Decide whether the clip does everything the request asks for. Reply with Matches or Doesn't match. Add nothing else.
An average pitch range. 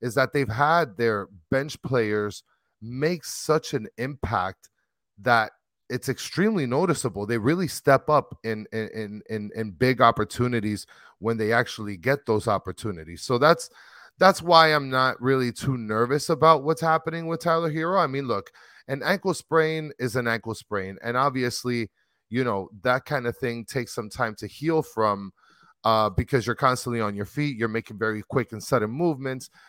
Matches